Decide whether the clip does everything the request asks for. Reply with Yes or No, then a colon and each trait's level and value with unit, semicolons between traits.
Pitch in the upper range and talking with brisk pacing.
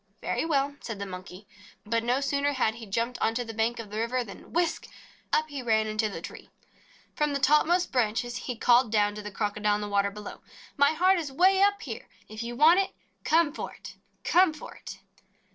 Yes: high, 240 Hz; fast, 210 wpm